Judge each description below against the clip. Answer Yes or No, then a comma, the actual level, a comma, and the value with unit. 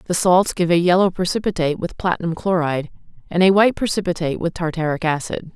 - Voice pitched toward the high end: No, medium, 175 Hz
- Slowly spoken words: No, average, 175 wpm